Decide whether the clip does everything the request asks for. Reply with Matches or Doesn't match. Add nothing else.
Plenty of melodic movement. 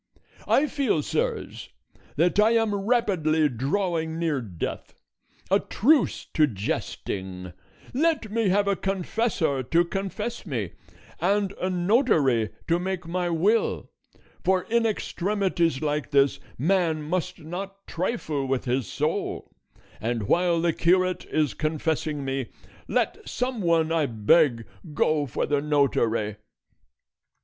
Matches